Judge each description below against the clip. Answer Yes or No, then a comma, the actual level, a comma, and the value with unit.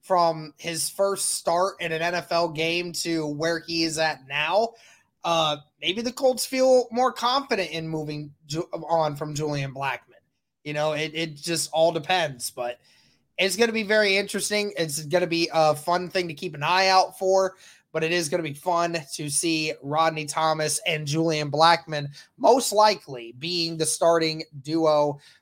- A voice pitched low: No, medium, 165 Hz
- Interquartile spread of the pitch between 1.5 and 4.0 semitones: Yes, average, 3.2 semitones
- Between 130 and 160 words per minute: No, average, 175 wpm